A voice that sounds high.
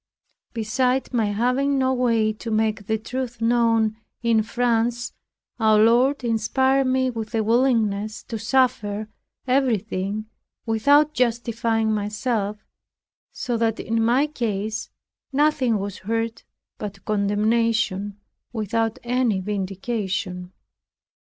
Yes: high, 225 Hz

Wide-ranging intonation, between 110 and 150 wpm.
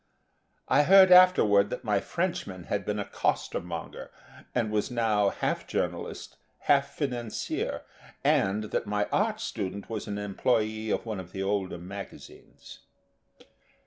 No: average, 3.8 semitones; slow, 135 wpm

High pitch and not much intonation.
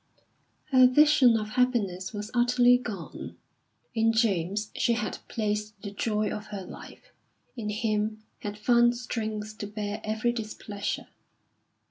Yes: high, 215 Hz; narrow, 2.3 semitones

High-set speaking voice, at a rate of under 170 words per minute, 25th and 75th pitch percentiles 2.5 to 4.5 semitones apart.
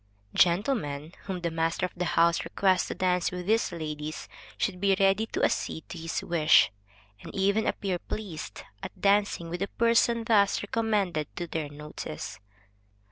No: medium, 180 Hz; average, 160 wpm; average, 3.7 semitones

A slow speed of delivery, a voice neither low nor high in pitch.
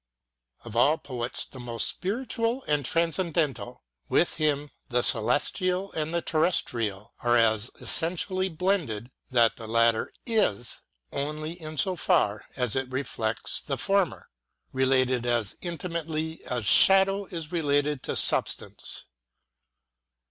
Yes: slow, 125 wpm; medium, 150 Hz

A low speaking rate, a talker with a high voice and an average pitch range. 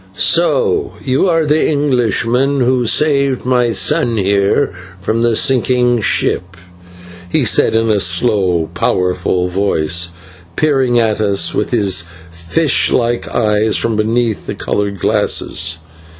No: slow, 125 wpm; low, 115 Hz; average, 4.7 semitones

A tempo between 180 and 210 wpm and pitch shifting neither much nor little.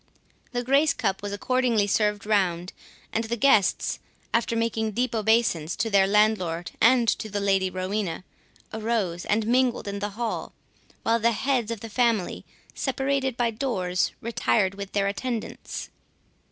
No: average, 150 wpm; average, 3.0 semitones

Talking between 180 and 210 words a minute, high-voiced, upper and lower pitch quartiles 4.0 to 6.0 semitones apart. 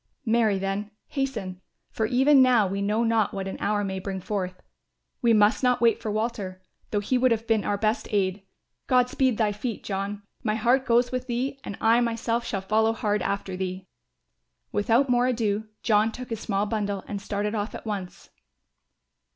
No: average, 185 wpm; high, 215 Hz; average, 2.9 semitones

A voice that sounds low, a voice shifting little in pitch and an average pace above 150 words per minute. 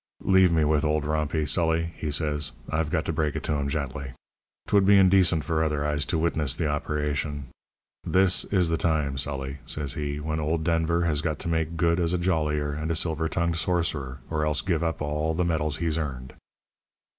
Yes: very low, 80 Hz; narrow, 2.1 semitones; fast, 205 wpm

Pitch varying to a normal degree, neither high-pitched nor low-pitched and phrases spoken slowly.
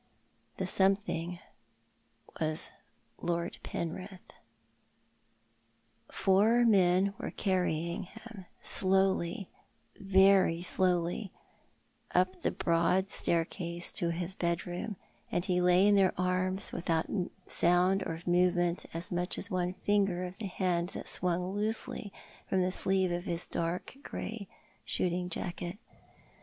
No: narrow, 1.8 semitones; medium, 180 Hz; slow, 125 wpm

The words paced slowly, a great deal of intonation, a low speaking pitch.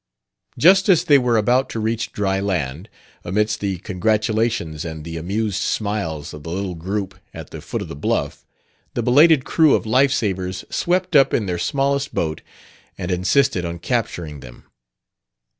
No: average, 165 wpm; wide, 6.1 semitones; low, 105 Hz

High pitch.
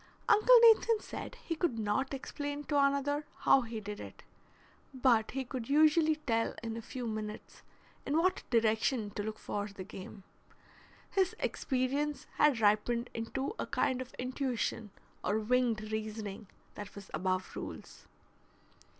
Yes: high, 245 Hz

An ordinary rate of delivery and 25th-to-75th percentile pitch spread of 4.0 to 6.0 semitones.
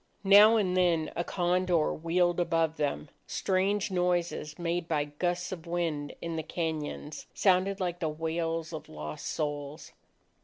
No: average, 145 wpm; narrow, 2.4 semitones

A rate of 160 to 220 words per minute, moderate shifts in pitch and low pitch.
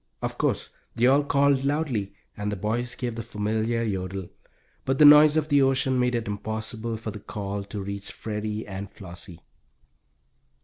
Yes: average, 170 wpm; average, 4.4 semitones; low, 110 Hz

